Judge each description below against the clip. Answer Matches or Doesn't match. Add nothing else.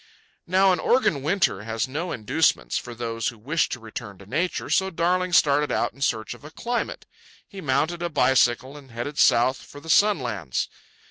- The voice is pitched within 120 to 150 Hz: Matches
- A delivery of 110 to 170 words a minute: Doesn't match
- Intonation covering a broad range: Matches